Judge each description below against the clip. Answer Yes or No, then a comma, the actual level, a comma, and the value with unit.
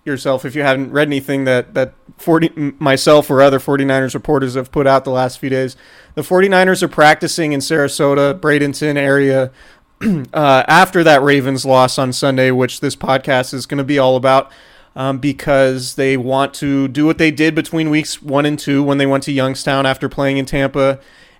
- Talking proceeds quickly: No, average, 190 wpm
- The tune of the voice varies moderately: No, narrow, 1.9 semitones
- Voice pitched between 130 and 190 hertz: Yes, medium, 140 Hz